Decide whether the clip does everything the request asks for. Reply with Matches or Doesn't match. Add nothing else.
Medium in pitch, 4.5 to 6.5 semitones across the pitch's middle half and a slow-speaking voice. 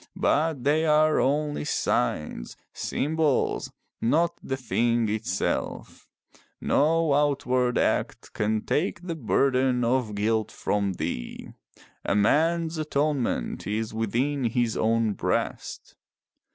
Doesn't match